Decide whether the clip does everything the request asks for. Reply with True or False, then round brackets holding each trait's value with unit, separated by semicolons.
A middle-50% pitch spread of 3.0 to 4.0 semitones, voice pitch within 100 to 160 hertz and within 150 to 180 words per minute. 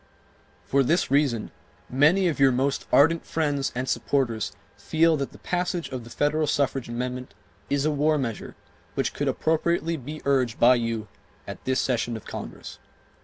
True (3.7 semitones; 140 Hz; 165 wpm)